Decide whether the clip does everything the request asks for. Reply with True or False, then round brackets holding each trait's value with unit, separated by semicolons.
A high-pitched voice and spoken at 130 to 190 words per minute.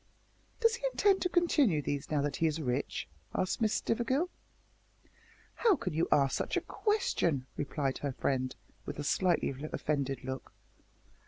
False (155 Hz; 155 wpm)